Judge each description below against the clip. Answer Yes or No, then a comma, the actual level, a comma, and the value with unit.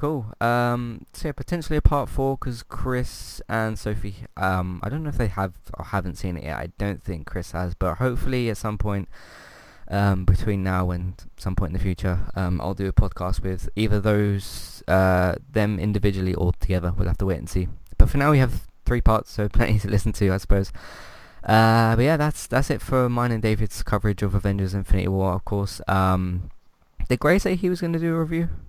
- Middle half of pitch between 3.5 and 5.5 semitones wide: Yes, average, 4.2 semitones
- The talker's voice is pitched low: Yes, low, 100 Hz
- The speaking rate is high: Yes, fast, 220 wpm